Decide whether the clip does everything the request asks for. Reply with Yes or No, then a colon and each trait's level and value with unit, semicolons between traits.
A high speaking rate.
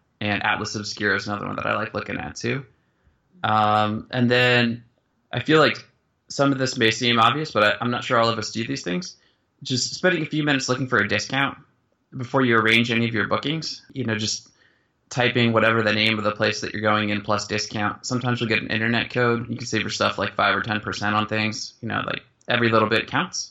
Yes: fast, 235 wpm